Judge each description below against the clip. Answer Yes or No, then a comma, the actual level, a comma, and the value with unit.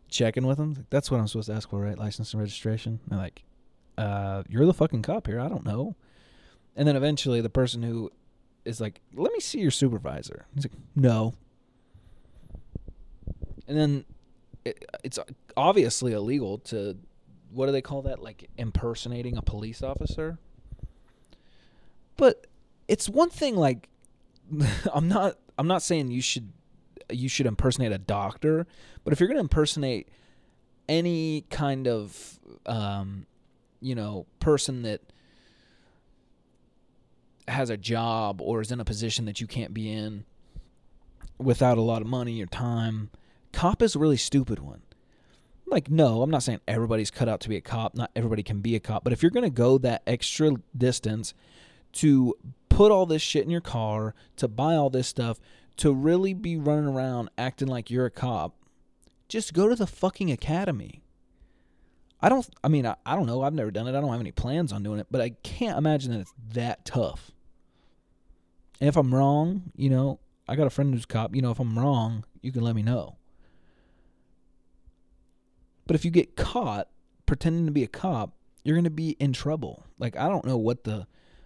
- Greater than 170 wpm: Yes, average, 180 wpm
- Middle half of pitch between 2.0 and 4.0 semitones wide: No, average, 5.2 semitones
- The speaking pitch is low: Yes, low, 120 Hz